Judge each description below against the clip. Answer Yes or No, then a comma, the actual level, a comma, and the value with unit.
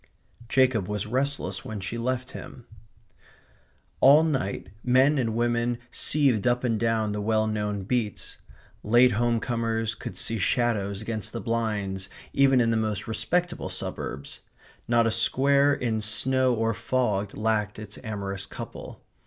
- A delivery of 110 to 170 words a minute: Yes, average, 145 wpm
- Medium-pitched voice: No, low, 115 Hz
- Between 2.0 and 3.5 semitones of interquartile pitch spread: Yes, average, 3.0 semitones